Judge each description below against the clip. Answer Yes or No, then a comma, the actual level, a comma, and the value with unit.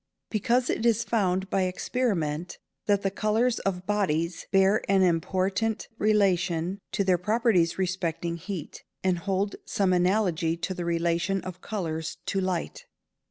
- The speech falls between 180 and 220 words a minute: No, average, 145 wpm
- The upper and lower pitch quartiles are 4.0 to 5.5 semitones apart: No, average, 3.1 semitones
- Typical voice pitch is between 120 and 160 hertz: No, high, 190 Hz